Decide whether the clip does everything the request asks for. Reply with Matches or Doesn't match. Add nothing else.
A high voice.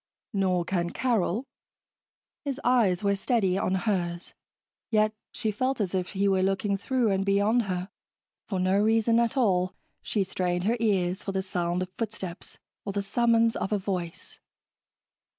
Matches